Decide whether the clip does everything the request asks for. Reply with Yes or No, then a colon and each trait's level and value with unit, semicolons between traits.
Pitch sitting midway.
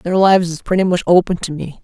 Yes: medium, 175 Hz